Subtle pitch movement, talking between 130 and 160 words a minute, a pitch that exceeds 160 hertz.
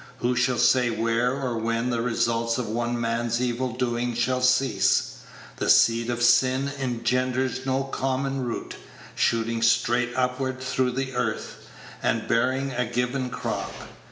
No: narrow, 1.6 semitones; average, 145 wpm; low, 125 Hz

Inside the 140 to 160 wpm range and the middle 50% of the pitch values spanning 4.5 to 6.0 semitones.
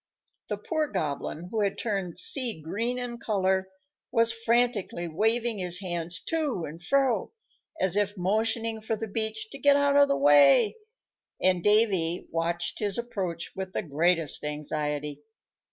Yes: average, 150 wpm; average, 5.2 semitones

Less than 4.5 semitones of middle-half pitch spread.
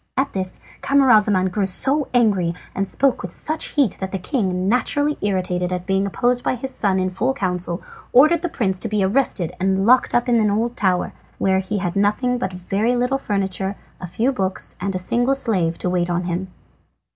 No: average, 5.0 semitones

